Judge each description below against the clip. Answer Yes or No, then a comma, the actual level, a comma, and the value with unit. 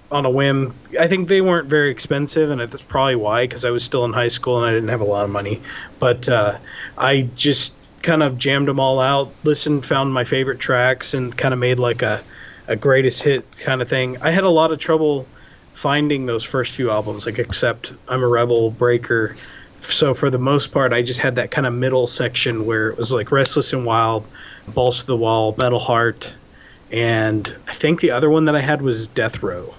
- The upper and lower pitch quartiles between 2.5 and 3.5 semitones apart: Yes, average, 3.0 semitones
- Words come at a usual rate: No, fast, 220 wpm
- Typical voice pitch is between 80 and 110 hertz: No, low, 130 Hz